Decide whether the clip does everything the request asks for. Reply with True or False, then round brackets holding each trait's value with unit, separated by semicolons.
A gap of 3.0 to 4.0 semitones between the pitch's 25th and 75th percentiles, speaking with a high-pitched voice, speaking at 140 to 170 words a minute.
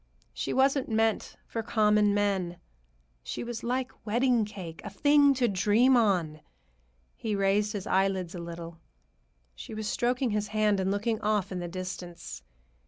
True (3.6 semitones; 210 Hz; 155 wpm)